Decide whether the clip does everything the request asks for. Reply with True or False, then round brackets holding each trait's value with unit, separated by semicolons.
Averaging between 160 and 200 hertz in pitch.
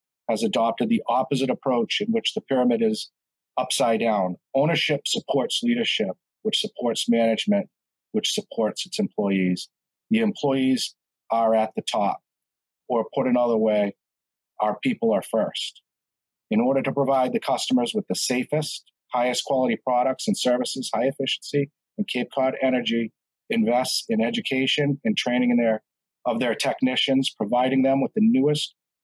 False (135 Hz)